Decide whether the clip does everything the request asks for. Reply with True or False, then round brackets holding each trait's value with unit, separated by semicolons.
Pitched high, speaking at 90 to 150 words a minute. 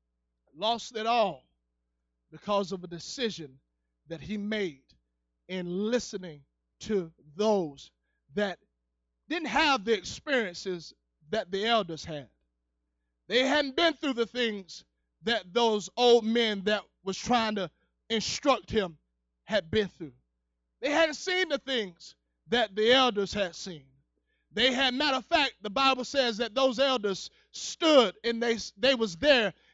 True (205 Hz; 140 wpm)